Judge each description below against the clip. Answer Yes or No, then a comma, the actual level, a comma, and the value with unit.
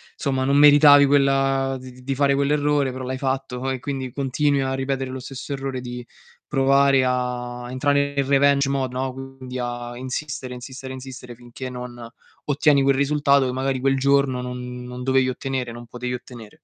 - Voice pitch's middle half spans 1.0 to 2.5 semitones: Yes, narrow, 1.7 semitones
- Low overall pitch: Yes, low, 130 Hz